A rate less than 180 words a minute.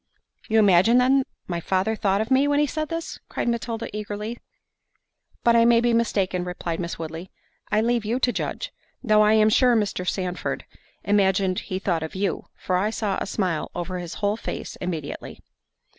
No: average, 185 wpm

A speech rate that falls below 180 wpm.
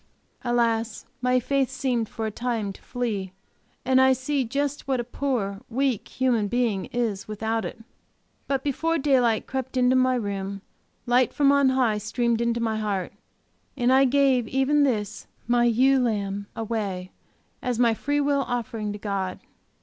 Yes: average, 160 wpm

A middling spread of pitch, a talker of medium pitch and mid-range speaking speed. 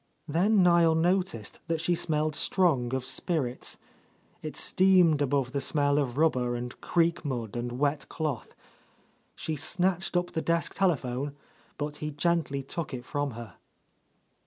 Yes: average, 4.5 semitones; medium, 150 Hz; average, 150 wpm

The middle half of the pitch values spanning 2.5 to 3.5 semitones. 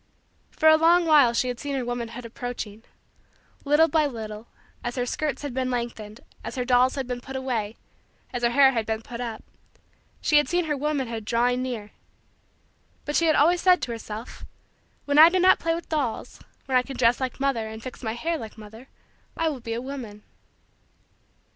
No: average, 4.1 semitones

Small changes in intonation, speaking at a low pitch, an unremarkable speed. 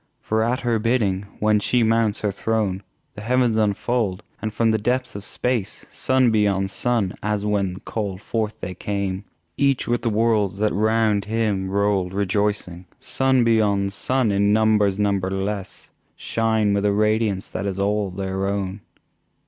Yes: narrow, 2.3 semitones; low, 105 Hz; average, 155 wpm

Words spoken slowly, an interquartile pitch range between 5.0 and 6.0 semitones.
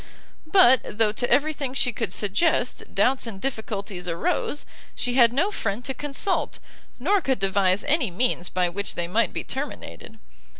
No: average, 165 wpm; wide, 5.5 semitones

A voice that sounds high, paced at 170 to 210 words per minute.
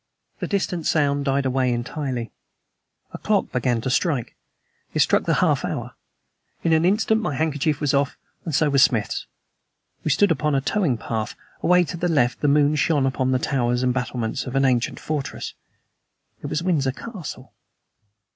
No: medium, 140 Hz; average, 175 wpm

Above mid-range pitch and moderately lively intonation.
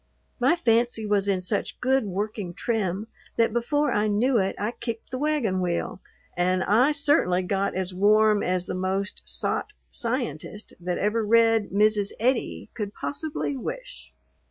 Yes: high, 215 Hz; average, 4.1 semitones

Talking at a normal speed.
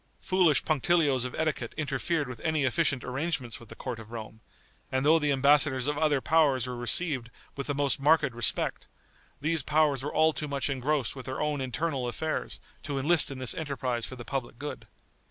Yes: average, 190 wpm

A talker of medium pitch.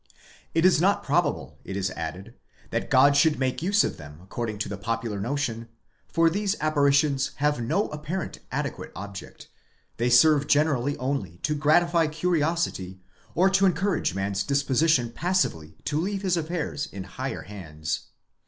Yes: medium, 145 Hz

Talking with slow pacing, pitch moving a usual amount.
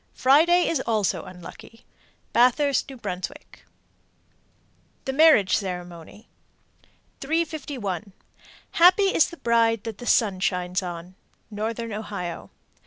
No: slow, 100 wpm; wide, 6.9 semitones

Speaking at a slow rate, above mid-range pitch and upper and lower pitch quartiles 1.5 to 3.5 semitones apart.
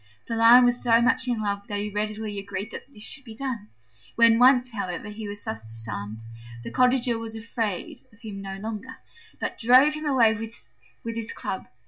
No: average, 190 wpm; high, 220 Hz; average, 3.2 semitones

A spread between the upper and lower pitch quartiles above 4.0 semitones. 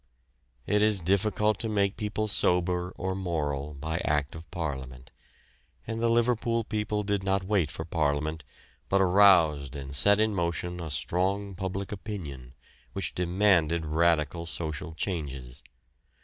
Yes: average, 4.8 semitones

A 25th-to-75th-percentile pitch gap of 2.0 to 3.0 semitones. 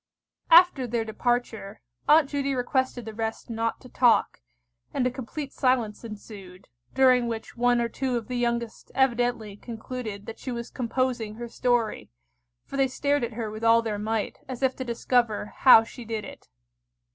Yes: narrow, 2.4 semitones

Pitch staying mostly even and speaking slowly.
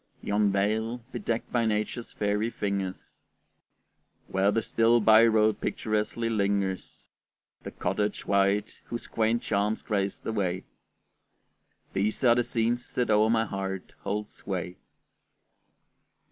Yes: narrow, 2.3 semitones; slow, 120 wpm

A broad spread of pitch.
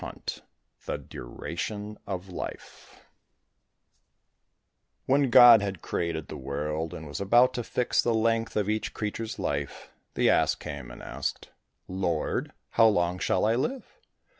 Yes: wide, 5.8 semitones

